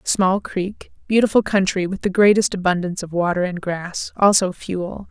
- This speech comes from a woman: Yes, female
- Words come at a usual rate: Yes, average, 155 wpm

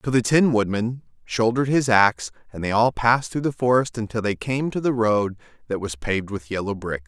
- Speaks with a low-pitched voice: Yes, low, 115 Hz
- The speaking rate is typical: No, fast, 220 wpm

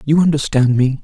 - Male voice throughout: Yes, male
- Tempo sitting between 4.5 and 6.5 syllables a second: Yes, 5.5 syllables/s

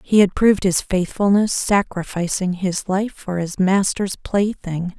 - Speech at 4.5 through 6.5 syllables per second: No, 4.1 syllables/s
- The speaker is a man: No, female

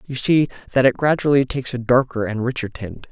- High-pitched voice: No, low, 125 Hz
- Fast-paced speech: Yes, fast, 210 wpm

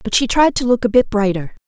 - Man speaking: No, female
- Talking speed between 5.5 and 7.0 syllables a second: Yes, 6.0 syllables/s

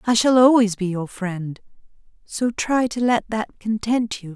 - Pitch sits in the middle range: No, high, 220 Hz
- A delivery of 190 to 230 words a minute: No, average, 180 wpm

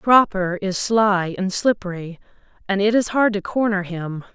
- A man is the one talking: No, female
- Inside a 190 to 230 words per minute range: No, average, 165 wpm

